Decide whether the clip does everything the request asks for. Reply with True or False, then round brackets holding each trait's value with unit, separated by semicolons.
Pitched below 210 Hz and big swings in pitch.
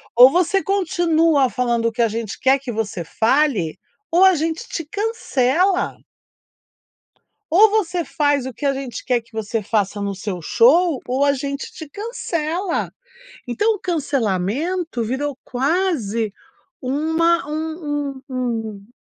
False (280 Hz; 6.3 semitones)